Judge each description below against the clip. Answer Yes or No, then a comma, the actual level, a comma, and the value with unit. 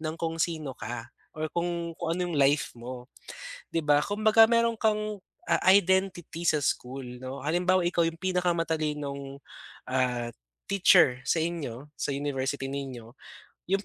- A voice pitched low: No, medium, 155 Hz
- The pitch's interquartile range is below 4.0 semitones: No, average, 4.6 semitones